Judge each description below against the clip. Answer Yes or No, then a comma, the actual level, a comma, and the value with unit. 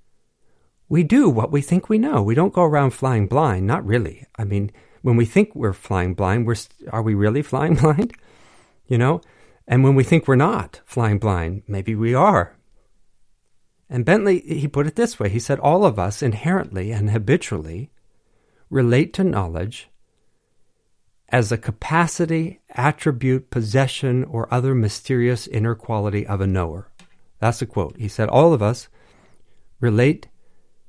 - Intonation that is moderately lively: No, wide, 5.7 semitones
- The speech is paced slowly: No, average, 160 wpm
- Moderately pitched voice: No, low, 120 Hz